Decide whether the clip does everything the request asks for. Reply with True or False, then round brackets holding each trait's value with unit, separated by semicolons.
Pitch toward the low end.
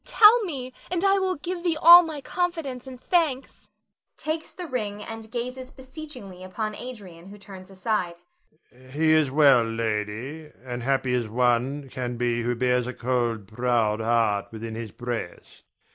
False (170 Hz)